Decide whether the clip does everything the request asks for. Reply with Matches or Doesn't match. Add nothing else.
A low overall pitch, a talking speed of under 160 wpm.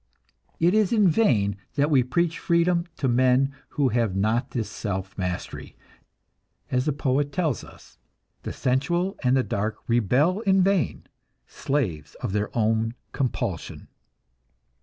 Matches